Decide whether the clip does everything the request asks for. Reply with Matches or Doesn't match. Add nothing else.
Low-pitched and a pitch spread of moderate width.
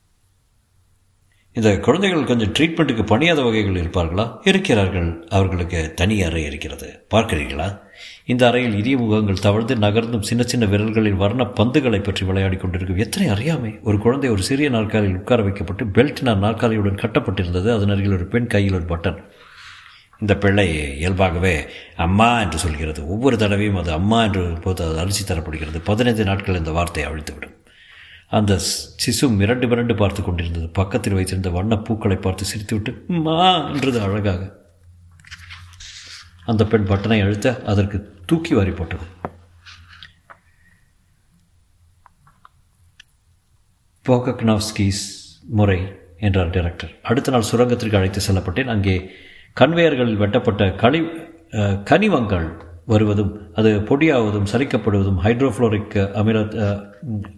Matches